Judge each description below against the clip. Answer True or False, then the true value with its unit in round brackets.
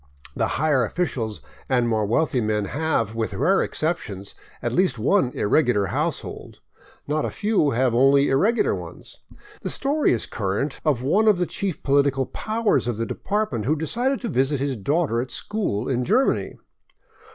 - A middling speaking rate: True (165 wpm)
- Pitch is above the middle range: False (140 Hz)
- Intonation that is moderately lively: False (7.3 semitones)